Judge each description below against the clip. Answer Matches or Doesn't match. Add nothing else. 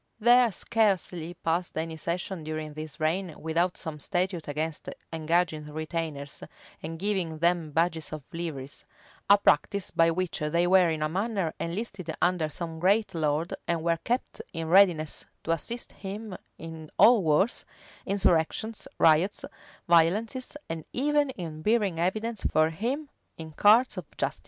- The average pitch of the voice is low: Doesn't match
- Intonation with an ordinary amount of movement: Matches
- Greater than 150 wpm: Doesn't match